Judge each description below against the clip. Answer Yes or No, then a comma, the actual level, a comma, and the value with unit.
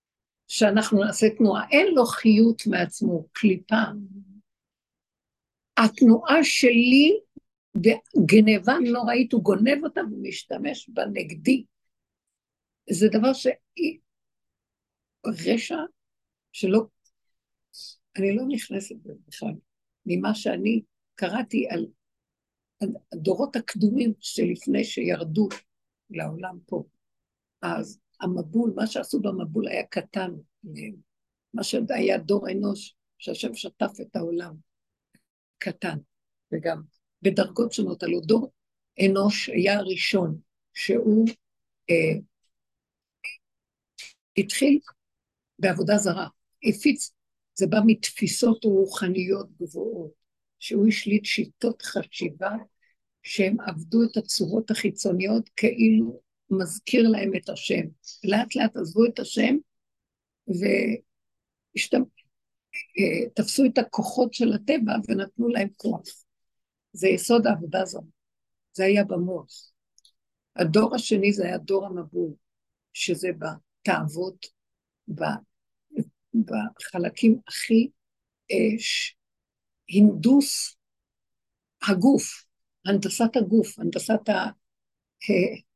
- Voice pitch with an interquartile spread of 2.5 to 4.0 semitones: Yes, average, 3.4 semitones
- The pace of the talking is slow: Yes, slow, 90 wpm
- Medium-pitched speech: No, high, 215 Hz